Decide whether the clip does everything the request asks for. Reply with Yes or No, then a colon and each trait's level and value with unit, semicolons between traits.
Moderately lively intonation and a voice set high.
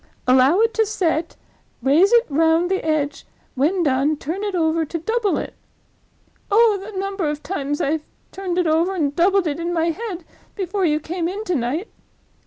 Yes: average, 4.2 semitones; very high, 340 Hz